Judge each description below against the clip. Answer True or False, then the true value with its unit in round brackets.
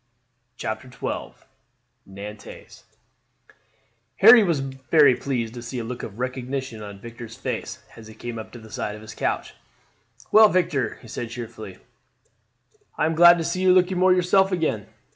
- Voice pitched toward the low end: True (125 Hz)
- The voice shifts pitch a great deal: True (7.4 semitones)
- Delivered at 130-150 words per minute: False (160 wpm)